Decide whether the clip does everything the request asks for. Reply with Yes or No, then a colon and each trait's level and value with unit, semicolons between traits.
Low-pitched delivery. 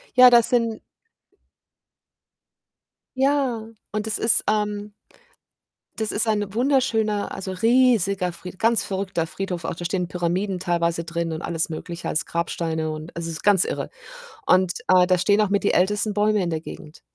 No: high, 195 Hz